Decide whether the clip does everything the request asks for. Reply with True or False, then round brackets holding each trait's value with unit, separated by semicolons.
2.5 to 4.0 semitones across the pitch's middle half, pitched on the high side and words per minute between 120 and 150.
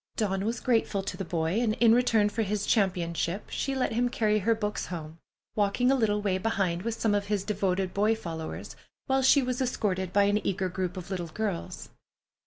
False (3.3 semitones; 205 Hz; 200 wpm)